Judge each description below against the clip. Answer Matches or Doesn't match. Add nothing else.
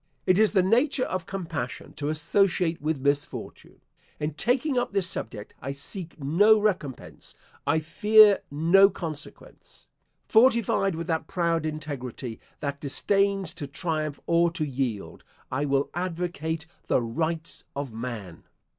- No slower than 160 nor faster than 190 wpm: Doesn't match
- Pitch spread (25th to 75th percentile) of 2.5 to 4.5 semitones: Doesn't match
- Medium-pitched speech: Matches